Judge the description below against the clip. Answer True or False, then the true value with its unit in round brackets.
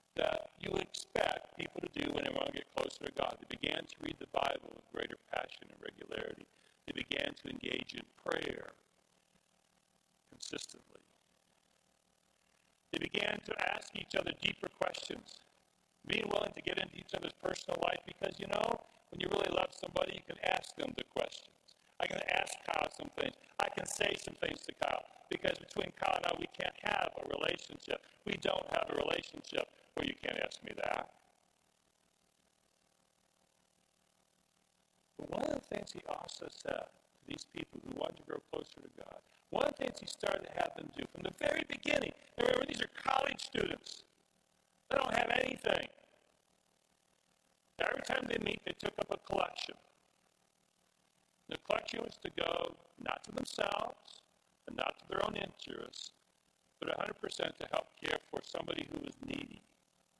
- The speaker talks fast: False (170 wpm)